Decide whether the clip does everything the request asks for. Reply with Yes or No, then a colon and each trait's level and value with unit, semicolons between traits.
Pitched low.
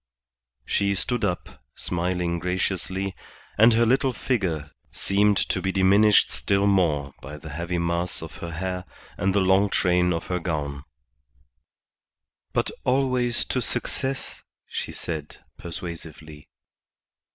Yes: very low, 90 Hz